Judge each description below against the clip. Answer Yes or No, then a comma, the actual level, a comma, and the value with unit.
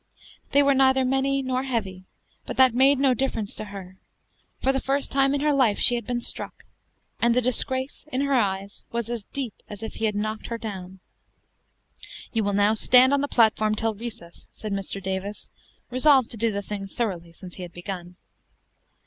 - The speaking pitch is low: No, high, 230 Hz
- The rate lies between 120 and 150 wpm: No, average, 195 wpm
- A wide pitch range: No, average, 4.7 semitones